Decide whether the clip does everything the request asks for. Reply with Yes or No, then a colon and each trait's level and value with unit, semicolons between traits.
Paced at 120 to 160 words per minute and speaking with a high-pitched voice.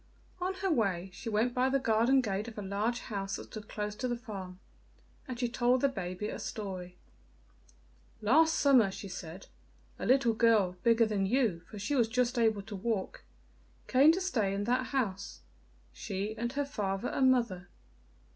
No: average, 180 wpm; high, 225 Hz